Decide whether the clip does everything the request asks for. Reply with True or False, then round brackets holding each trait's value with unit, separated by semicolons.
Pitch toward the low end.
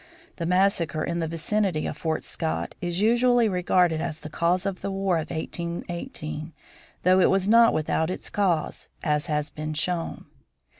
False (170 Hz)